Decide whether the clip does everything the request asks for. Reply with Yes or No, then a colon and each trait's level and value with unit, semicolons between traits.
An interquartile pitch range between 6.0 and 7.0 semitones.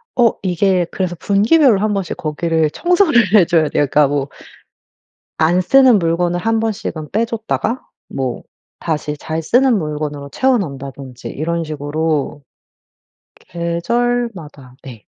Yes: wide, 6.7 semitones